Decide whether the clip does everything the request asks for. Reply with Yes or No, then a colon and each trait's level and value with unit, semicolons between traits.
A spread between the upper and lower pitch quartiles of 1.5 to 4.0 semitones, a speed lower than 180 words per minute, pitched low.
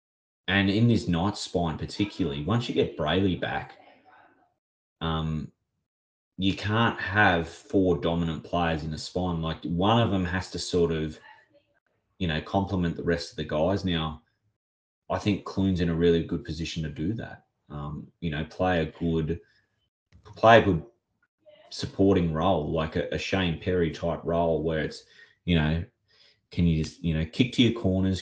Yes: average, 3.4 semitones; average, 170 wpm; very low, 85 Hz